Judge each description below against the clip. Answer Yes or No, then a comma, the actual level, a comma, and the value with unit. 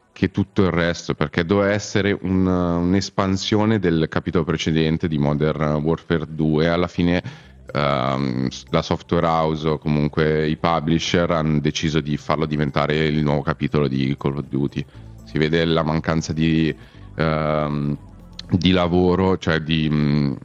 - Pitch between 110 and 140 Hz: No, very low, 80 Hz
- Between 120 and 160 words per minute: Yes, average, 145 wpm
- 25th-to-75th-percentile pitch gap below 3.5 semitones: Yes, average, 2.8 semitones